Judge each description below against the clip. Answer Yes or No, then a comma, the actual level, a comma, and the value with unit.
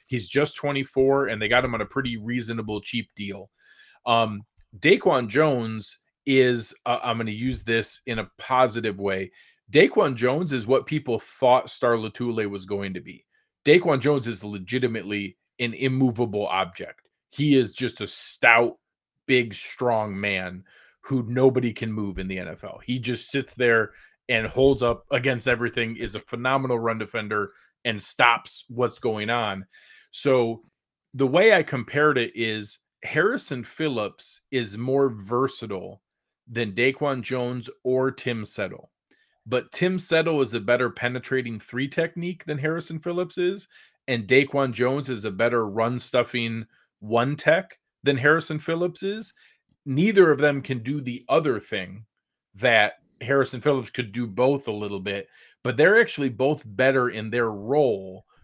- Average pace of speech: Yes, average, 155 wpm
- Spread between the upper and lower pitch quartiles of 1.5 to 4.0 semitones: Yes, average, 3.4 semitones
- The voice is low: Yes, low, 125 Hz